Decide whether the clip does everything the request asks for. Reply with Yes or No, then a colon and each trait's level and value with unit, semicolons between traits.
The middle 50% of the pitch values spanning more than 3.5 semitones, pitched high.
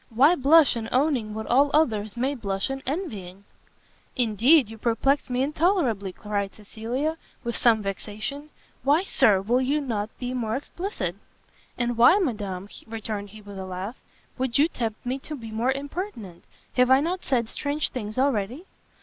Yes: average, 5.0 semitones; high, 240 Hz